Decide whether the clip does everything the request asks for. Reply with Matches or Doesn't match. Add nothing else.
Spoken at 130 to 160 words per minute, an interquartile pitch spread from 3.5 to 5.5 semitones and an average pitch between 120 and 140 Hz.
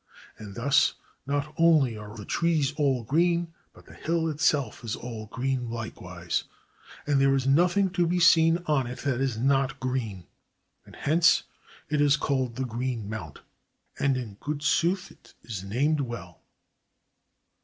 Matches